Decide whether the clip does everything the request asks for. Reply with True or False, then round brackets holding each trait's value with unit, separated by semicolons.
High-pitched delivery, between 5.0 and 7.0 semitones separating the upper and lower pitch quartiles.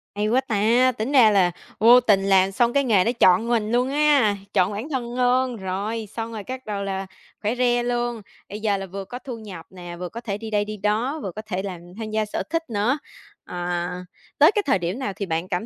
False (215 Hz; 3.9 semitones)